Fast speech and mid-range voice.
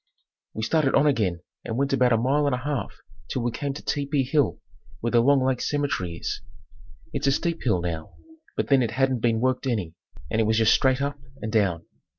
No: fast, 215 wpm; low, 125 Hz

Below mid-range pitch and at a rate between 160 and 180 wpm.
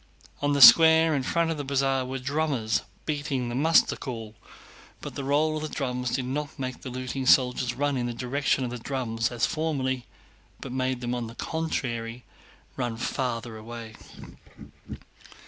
Yes: low, 130 Hz; average, 170 wpm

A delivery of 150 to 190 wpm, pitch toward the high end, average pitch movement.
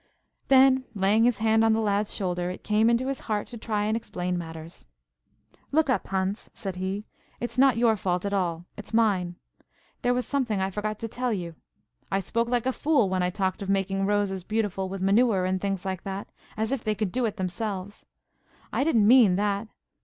No: average, 200 wpm; high, 205 Hz; average, 3.4 semitones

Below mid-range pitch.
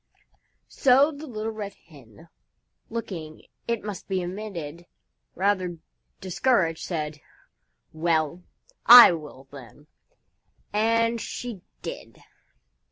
No: medium, 185 Hz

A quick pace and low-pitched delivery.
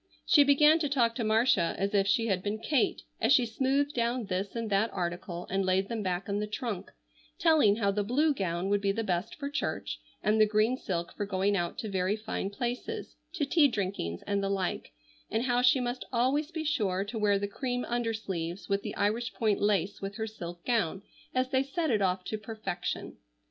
No: fast, 210 wpm; high, 215 Hz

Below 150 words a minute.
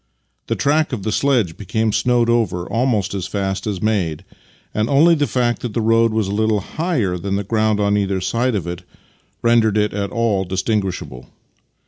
No: average, 185 wpm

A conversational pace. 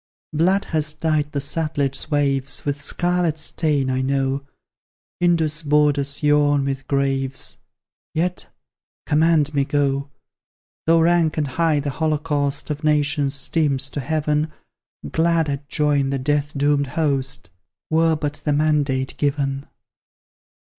No: slow, 125 wpm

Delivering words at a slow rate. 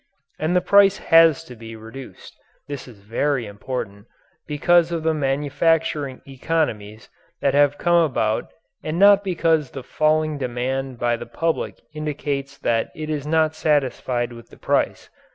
No: average, 150 wpm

